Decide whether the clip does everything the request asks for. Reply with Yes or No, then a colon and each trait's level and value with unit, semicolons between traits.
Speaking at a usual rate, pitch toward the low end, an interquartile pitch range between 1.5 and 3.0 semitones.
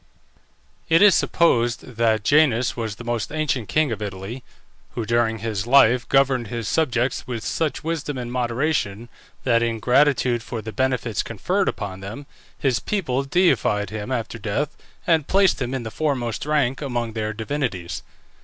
No: average, 160 wpm; low, 120 Hz; average, 3.9 semitones